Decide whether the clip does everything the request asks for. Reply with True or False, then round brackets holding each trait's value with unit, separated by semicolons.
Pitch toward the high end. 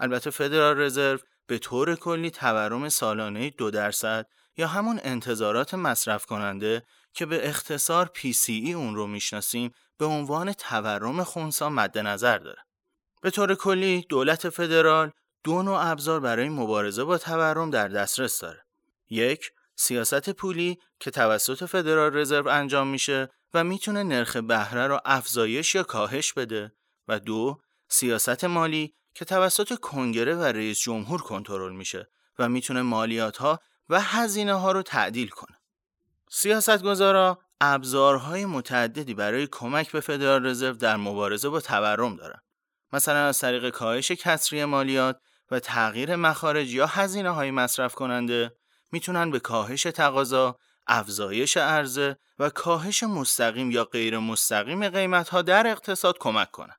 False (140 Hz)